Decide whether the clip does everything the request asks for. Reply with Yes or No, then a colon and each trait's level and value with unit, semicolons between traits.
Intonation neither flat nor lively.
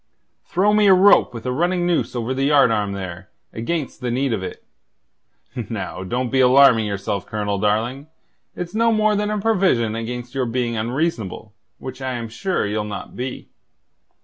No: wide, 7.3 semitones